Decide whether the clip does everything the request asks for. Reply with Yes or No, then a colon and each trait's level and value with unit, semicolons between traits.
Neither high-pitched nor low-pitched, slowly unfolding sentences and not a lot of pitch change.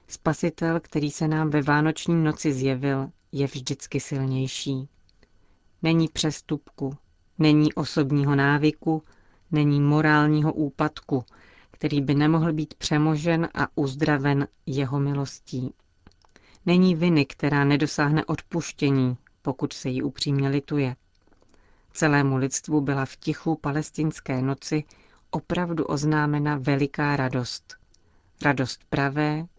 Yes: medium, 145 Hz; slow, 105 wpm; narrow, 2.0 semitones